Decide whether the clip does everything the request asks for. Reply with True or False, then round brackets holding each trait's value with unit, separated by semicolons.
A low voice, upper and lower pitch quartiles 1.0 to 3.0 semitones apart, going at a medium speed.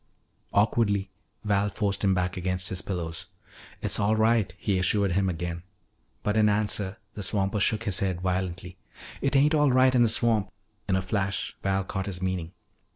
True (100 Hz; 2.6 semitones; 175 wpm)